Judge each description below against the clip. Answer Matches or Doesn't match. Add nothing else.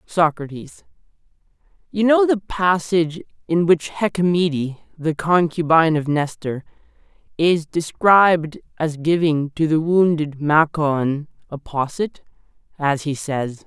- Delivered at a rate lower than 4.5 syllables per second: Matches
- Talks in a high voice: Doesn't match